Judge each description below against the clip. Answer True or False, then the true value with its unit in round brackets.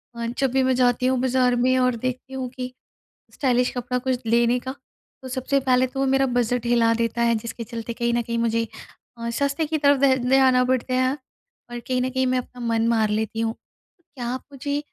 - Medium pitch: False (250 Hz)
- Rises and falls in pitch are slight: True (1.7 semitones)